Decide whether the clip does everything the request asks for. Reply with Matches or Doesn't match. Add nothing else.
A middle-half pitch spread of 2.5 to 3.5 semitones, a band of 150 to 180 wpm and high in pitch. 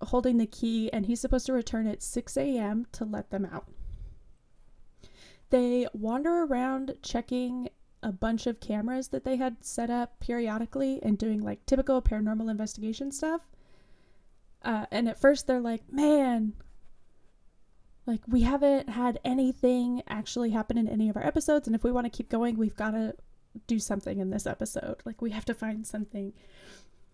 Matches